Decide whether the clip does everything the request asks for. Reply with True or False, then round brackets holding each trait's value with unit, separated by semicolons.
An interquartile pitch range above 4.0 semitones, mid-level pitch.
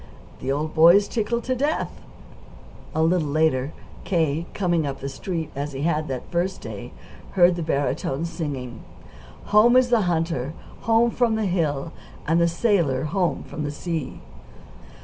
True (4.8 semitones; 165 Hz)